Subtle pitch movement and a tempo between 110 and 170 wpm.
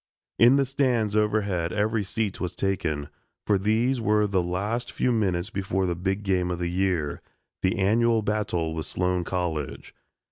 No: average, 3.3 semitones; average, 165 wpm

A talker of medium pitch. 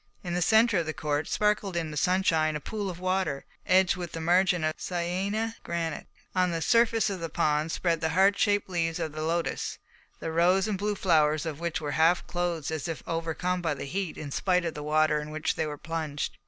Yes: medium, 170 Hz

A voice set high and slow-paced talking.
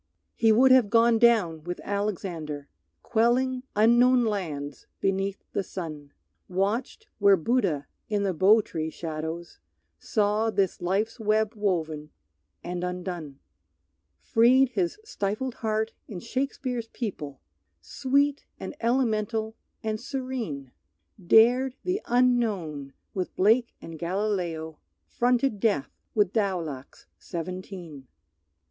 Yes: high, 205 Hz; slow, 110 wpm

